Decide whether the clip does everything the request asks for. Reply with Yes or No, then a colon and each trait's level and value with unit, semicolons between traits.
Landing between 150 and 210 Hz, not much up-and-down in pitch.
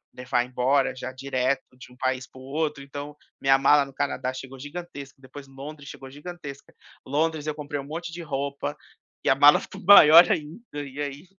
No: medium, 140 Hz; narrow, 2.0 semitones